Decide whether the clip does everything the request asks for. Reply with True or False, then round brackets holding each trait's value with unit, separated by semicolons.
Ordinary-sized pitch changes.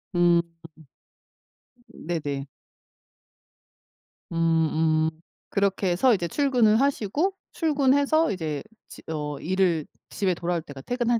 False (7.4 semitones)